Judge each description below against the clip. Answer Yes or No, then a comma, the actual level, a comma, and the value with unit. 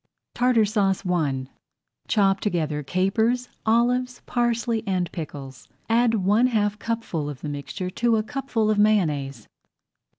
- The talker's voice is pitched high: Yes, high, 205 Hz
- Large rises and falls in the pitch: Yes, wide, 5.9 semitones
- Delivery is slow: Yes, slow, 130 wpm